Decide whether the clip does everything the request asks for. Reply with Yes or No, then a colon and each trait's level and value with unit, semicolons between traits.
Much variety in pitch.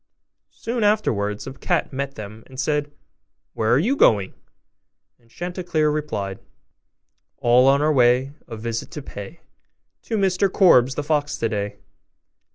Yes: wide, 5.9 semitones